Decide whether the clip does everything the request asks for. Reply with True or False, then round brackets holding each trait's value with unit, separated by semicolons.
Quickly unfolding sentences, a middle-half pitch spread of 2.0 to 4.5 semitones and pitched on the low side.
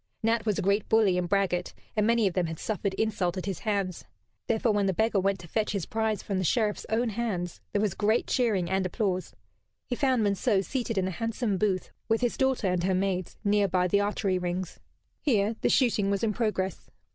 False (215 wpm; 2.9 semitones; 200 Hz)